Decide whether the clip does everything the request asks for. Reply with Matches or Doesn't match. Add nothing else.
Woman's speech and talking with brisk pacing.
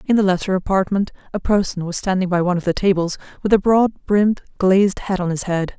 Matches